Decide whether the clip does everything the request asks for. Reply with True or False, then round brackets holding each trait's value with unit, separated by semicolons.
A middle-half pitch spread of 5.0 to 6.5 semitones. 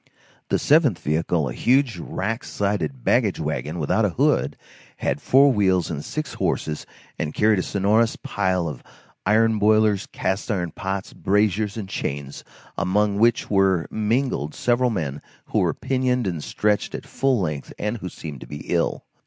True (5.3 semitones)